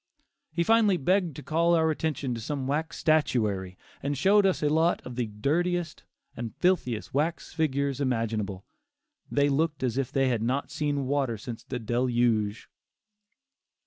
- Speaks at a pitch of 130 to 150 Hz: Yes, medium, 140 Hz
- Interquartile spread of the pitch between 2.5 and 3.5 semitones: No, average, 5.1 semitones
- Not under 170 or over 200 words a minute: No, average, 155 wpm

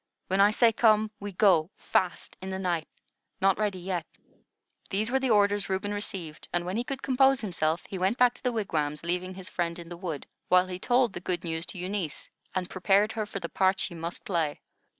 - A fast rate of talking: Yes, fast, 215 wpm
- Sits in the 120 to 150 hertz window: No, high, 190 Hz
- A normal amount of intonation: Yes, average, 3.3 semitones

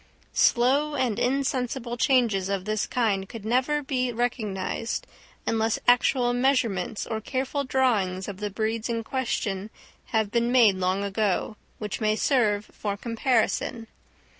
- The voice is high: Yes, high, 230 Hz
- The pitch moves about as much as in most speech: Yes, average, 3.5 semitones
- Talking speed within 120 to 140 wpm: Yes, slow, 135 wpm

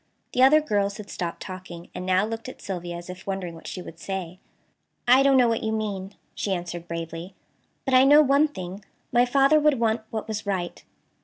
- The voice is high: Yes, high, 200 Hz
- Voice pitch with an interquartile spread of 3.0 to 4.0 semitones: No, wide, 5.6 semitones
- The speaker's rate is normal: No, fast, 210 wpm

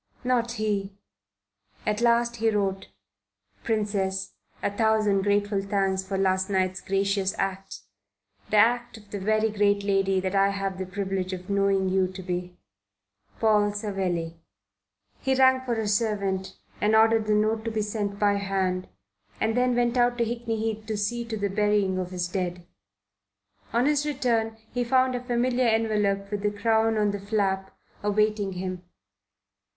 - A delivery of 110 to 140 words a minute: No, average, 160 wpm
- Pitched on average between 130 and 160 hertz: No, high, 205 Hz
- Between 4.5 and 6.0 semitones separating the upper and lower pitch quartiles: No, narrow, 2.5 semitones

